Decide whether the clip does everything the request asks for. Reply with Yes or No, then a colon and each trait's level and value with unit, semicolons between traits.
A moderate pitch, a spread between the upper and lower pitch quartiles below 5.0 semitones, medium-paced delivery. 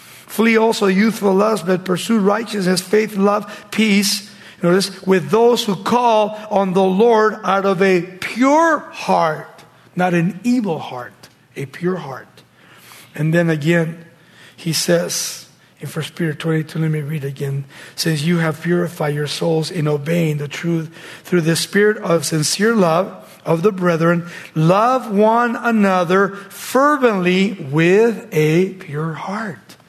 Yes: medium, 180 Hz; average, 4.3 semitones; average, 145 wpm